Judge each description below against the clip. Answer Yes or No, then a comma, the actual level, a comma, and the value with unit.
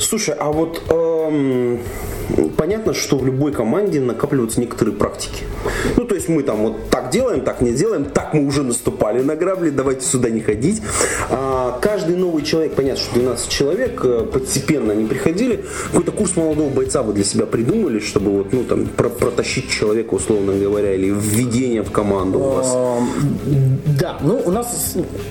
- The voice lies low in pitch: Yes, low, 130 Hz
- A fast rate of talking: Yes, fast, 165 wpm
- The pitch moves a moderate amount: No, wide, 5.9 semitones